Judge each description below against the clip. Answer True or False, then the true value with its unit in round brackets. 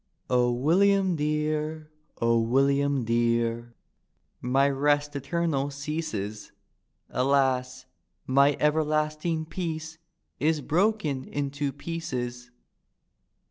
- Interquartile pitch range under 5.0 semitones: True (3.6 semitones)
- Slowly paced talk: True (80 wpm)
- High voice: False (140 Hz)